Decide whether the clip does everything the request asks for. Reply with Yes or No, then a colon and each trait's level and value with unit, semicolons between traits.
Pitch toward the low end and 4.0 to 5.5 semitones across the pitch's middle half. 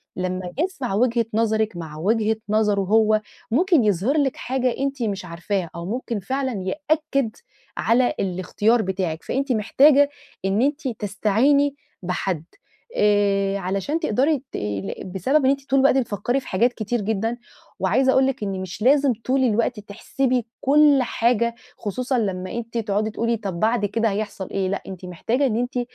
No: high, 225 Hz; average, 4.9 semitones